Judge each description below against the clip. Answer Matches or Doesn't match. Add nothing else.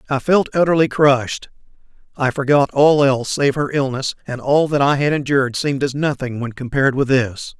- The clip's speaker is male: Matches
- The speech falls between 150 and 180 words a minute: Doesn't match